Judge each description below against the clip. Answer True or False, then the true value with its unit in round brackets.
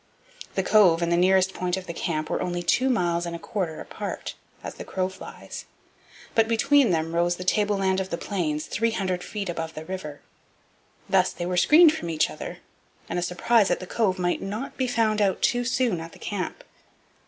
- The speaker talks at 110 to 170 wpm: False (200 wpm)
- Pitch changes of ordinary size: True (3.7 semitones)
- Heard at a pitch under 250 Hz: True (185 Hz)